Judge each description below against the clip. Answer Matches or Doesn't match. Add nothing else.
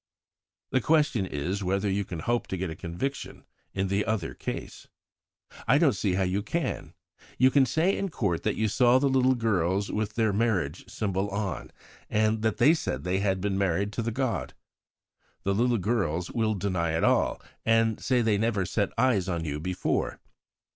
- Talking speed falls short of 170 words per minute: Doesn't match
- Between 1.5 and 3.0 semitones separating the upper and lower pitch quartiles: Doesn't match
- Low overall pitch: Matches